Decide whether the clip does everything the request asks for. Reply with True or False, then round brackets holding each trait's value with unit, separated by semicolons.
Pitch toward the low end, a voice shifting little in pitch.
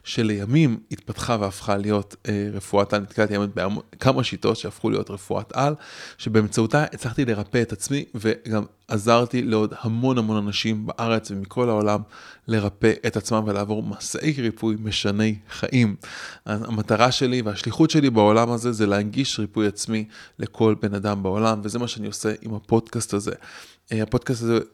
True (110 Hz; 2.3 semitones)